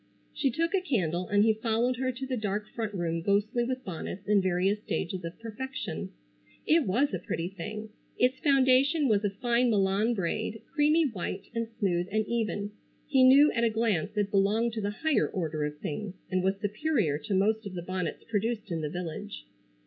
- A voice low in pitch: No, high, 210 Hz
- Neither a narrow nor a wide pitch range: Yes, average, 4.6 semitones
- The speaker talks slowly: No, average, 195 wpm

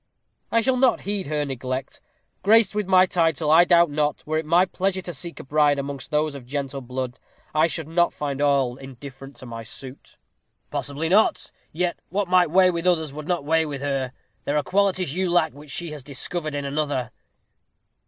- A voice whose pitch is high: No, medium, 150 Hz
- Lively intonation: No, average, 4.1 semitones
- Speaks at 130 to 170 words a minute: No, average, 195 wpm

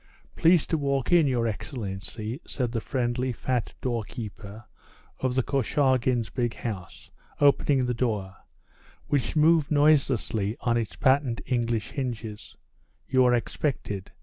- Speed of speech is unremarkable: No, slow, 125 wpm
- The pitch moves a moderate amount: Yes, average, 3.4 semitones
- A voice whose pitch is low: Yes, low, 125 Hz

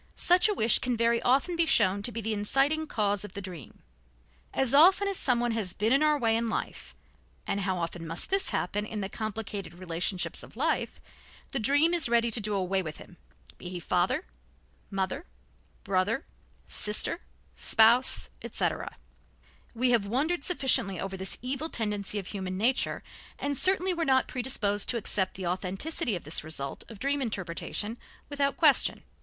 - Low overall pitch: No, high, 220 Hz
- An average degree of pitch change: No, wide, 5.9 semitones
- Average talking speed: Yes, average, 170 wpm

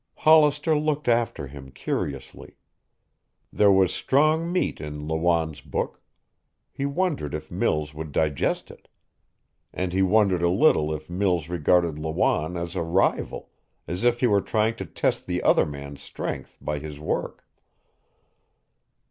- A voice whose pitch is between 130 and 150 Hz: No, very low, 85 Hz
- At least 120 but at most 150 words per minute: Yes, average, 140 wpm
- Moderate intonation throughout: No, wide, 7.4 semitones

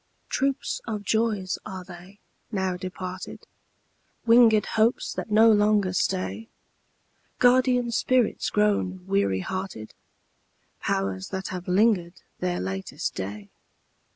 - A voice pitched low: No, high, 190 Hz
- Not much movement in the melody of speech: No, average, 3.5 semitones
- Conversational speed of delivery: No, slow, 105 wpm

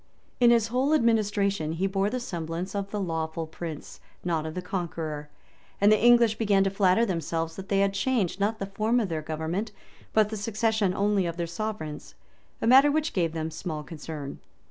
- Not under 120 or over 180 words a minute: No, average, 190 wpm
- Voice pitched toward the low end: No, high, 195 Hz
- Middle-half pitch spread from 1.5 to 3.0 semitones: No, average, 4.9 semitones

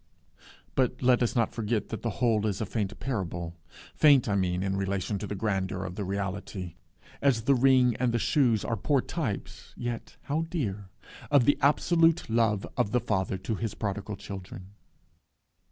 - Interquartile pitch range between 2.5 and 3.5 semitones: No, average, 4.3 semitones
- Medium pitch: No, low, 110 Hz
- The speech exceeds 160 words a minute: Yes, average, 175 wpm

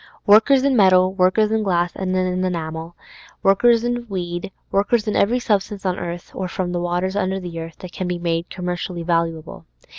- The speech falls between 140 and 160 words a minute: No, average, 185 wpm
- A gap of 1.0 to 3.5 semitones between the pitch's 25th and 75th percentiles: Yes, average, 2.8 semitones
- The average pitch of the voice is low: No, medium, 185 Hz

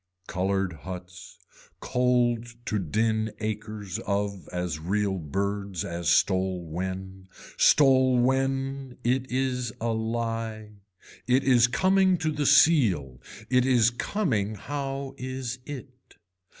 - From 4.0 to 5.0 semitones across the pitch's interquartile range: No, wide, 5.4 semitones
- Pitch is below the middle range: Yes, low, 115 Hz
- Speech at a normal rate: No, slow, 110 wpm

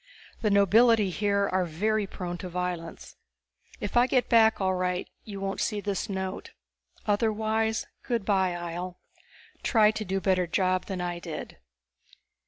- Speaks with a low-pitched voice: No, high, 195 Hz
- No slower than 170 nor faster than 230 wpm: No, average, 155 wpm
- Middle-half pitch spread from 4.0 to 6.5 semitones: No, average, 3.0 semitones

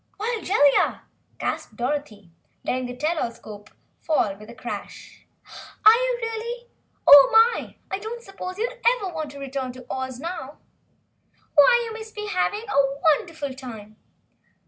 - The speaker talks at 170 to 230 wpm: No, average, 150 wpm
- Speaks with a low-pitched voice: No, very high, 300 Hz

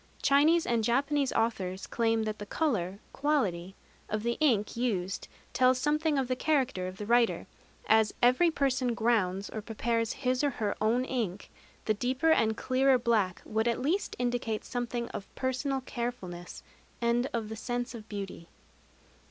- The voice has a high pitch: Yes, high, 235 Hz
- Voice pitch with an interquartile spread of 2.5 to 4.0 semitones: Yes, average, 3.4 semitones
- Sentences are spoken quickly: No, average, 160 wpm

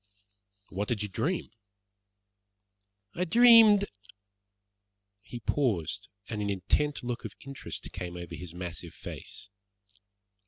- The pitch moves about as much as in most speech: No, wide, 8.1 semitones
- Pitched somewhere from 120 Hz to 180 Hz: No, low, 110 Hz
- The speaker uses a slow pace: Yes, slow, 115 wpm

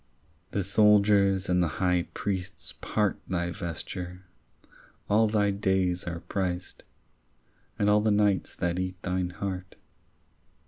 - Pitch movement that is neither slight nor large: No, narrow, 2.3 semitones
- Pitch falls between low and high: No, very low, 95 Hz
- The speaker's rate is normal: No, slow, 125 wpm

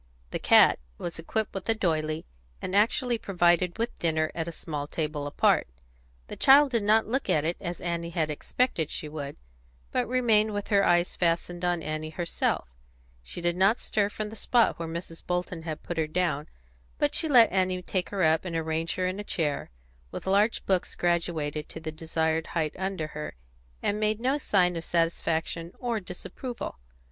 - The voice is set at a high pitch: No, medium, 175 Hz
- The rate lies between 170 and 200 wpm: Yes, average, 185 wpm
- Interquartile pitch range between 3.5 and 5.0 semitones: Yes, average, 4.2 semitones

